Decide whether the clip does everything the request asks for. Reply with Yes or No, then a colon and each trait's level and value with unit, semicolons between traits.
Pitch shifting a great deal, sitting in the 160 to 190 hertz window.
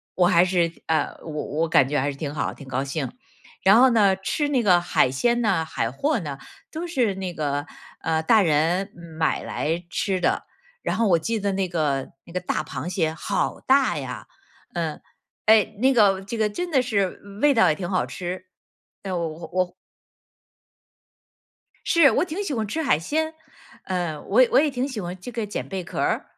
Yes: wide, 6.1 semitones; medium, 185 Hz